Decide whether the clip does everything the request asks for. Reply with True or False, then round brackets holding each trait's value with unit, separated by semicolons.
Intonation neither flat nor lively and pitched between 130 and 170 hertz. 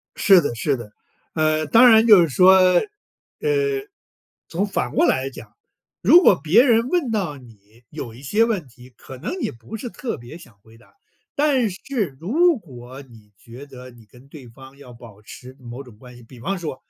False (8.8 semitones; 140 Hz)